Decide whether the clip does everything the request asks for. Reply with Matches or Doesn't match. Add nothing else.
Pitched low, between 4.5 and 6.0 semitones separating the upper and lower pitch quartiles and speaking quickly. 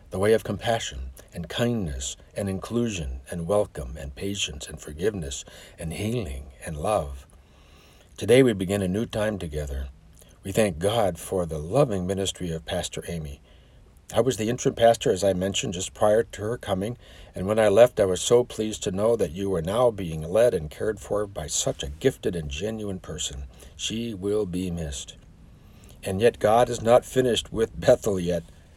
Doesn't match